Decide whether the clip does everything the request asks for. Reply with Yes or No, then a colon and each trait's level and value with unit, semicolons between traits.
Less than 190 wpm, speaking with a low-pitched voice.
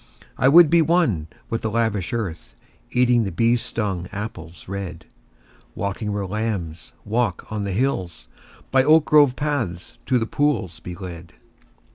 Yes: average, 150 wpm; low, 105 Hz